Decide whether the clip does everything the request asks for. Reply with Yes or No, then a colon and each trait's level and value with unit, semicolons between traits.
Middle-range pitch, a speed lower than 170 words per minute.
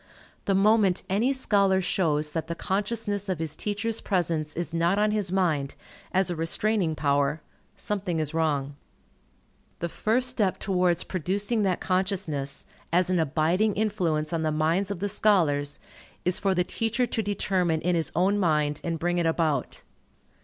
Yes: medium, 180 Hz; average, 160 wpm